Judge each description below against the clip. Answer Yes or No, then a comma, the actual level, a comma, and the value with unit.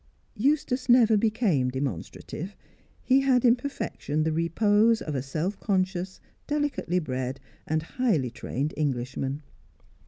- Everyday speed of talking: No, slow, 120 wpm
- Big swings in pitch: Yes, wide, 8.8 semitones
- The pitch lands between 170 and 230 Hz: Yes, medium, 185 Hz